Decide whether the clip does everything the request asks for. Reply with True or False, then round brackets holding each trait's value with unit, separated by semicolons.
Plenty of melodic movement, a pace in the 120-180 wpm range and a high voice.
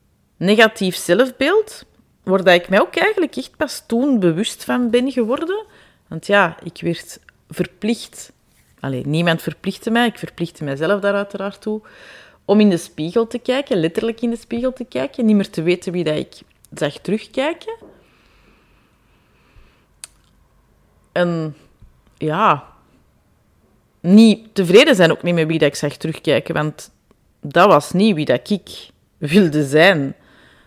True (6.0 semitones; 140 wpm; 200 Hz)